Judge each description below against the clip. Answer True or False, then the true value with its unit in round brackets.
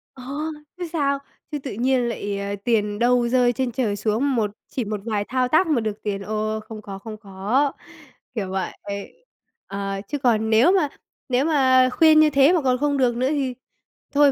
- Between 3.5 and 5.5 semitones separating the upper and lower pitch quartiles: True (4.4 semitones)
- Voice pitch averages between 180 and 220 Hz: False (245 Hz)